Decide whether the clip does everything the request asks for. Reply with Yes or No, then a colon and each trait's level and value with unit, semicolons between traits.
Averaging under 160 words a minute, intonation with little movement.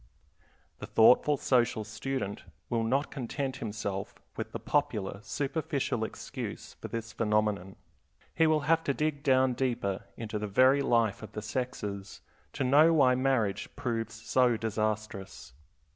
No: average, 140 wpm; average, 4.1 semitones